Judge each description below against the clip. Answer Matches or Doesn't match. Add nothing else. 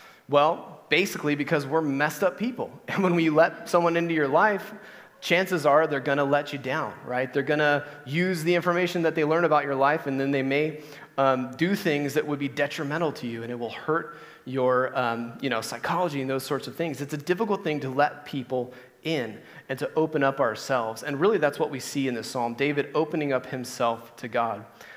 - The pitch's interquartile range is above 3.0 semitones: Matches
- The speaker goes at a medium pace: Doesn't match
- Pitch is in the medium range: Matches